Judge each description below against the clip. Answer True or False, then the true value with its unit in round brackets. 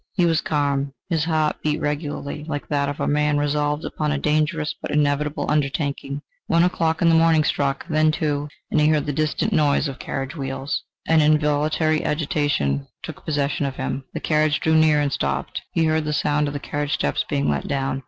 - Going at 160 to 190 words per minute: False (200 wpm)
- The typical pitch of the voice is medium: True (150 Hz)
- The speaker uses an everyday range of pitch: False (1.5 semitones)